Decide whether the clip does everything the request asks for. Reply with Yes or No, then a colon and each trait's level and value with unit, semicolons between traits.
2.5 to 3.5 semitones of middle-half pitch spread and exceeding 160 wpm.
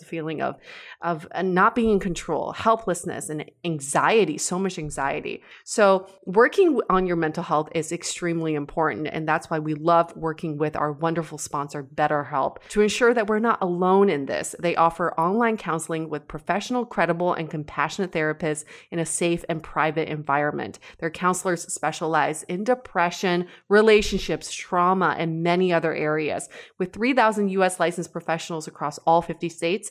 No: average, 2.9 semitones; average, 155 wpm